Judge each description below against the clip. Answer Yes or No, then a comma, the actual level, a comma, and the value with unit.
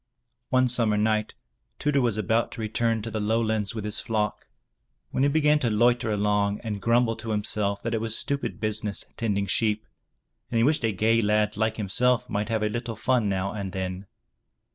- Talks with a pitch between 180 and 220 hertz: No, low, 110 Hz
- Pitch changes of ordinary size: No, narrow, 1.9 semitones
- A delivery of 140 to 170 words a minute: No, average, 195 wpm